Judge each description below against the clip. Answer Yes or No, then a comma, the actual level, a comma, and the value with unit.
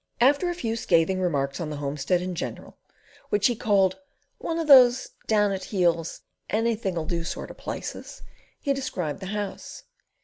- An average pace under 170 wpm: No, average, 175 wpm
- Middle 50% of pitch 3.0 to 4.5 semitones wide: No, wide, 5.4 semitones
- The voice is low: No, high, 190 Hz